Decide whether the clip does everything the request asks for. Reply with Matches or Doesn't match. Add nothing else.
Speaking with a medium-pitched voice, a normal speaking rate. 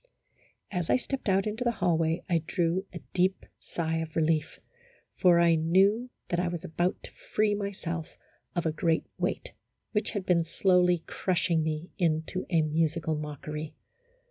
Matches